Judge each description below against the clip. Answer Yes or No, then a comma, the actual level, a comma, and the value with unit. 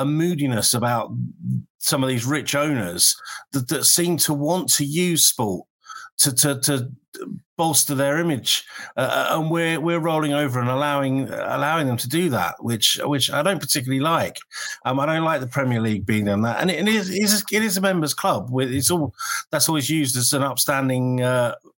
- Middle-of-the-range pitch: Yes, medium, 145 Hz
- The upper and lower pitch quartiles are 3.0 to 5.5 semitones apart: Yes, average, 4.4 semitones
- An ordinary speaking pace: Yes, average, 190 wpm